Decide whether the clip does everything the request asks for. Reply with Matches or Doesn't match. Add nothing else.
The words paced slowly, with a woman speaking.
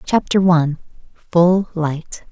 Matches